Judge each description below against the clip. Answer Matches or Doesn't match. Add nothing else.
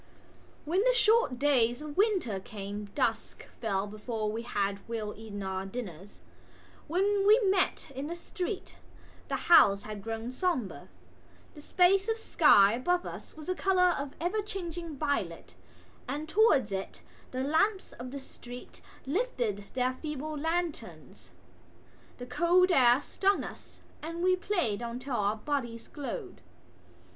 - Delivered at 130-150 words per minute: Matches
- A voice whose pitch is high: Matches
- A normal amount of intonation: Doesn't match